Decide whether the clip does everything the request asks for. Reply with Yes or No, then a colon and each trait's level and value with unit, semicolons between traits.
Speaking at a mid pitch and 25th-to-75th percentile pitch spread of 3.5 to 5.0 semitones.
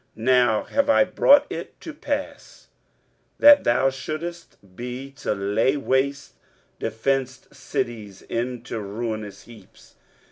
No: low, 125 Hz; average, 4.1 semitones